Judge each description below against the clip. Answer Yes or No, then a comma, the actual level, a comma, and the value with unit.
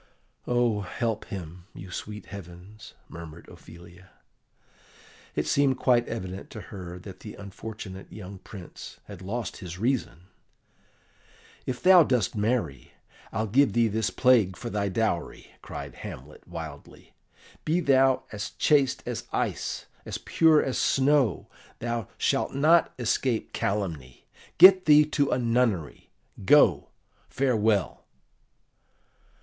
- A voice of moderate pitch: No, low, 110 Hz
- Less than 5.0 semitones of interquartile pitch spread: No, wide, 5.5 semitones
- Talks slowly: Yes, slow, 120 wpm